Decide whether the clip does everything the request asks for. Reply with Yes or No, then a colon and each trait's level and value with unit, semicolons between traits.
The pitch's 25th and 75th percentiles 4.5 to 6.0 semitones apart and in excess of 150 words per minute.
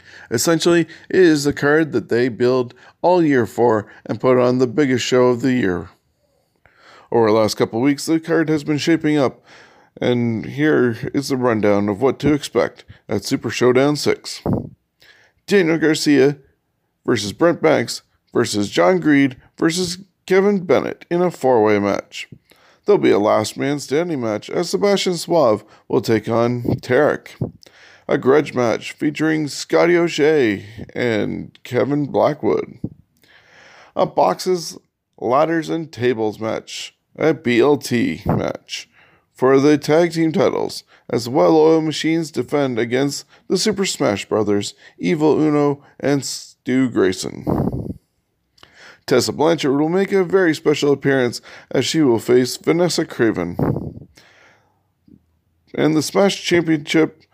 No: average, 4.9 semitones; slow, 135 wpm